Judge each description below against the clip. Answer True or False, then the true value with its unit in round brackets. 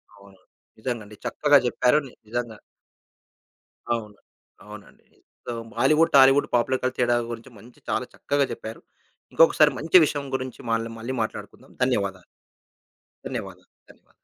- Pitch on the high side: False (120 Hz)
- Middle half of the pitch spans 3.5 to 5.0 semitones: True (3.8 semitones)